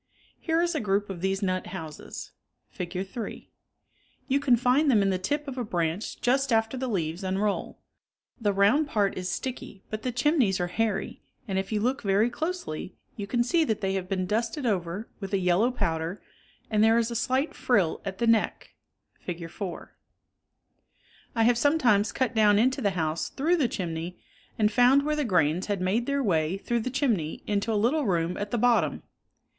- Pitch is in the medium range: No, high, 210 Hz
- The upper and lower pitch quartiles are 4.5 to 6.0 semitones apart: Yes, average, 4.9 semitones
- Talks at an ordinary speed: Yes, average, 195 wpm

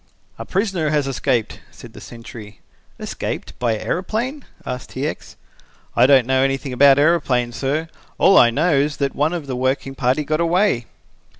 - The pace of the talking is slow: No, average, 170 wpm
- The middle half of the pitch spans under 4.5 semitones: Yes, average, 4.1 semitones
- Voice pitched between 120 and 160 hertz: Yes, medium, 140 Hz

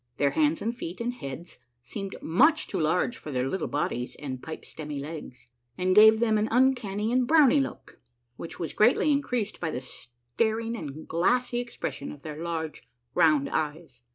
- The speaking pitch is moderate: Yes, medium, 175 Hz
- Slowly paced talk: No, average, 180 wpm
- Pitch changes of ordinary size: No, wide, 7.7 semitones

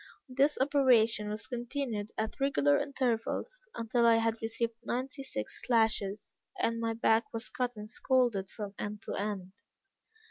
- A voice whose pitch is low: No, high, 230 Hz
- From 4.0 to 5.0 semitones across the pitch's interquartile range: No, average, 3.2 semitones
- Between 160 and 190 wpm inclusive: No, average, 145 wpm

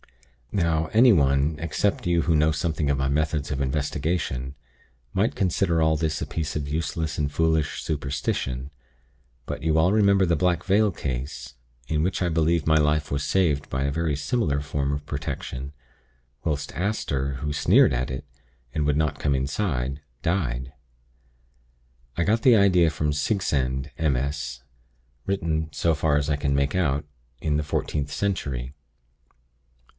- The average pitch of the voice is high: No, very low, 75 Hz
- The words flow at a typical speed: Yes, average, 155 wpm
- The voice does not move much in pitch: No, average, 3.1 semitones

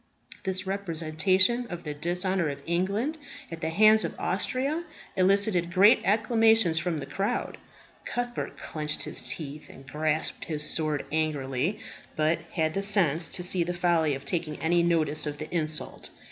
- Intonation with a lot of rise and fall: No, average, 4.1 semitones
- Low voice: No, medium, 170 Hz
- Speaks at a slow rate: No, average, 155 wpm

